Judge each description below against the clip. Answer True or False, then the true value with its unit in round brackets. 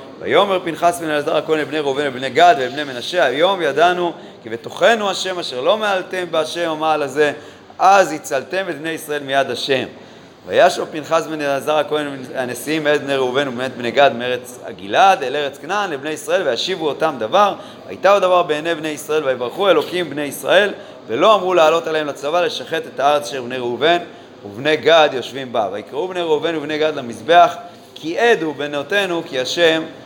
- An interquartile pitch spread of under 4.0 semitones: True (3.6 semitones)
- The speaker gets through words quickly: True (160 wpm)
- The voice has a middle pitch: True (155 Hz)